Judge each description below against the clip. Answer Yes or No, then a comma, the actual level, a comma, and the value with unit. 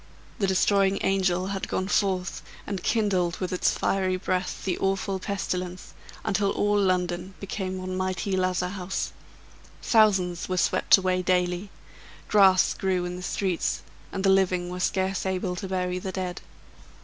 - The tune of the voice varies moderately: No, narrow, 1.2 semitones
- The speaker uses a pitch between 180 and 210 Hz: Yes, medium, 185 Hz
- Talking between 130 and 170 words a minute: Yes, average, 150 wpm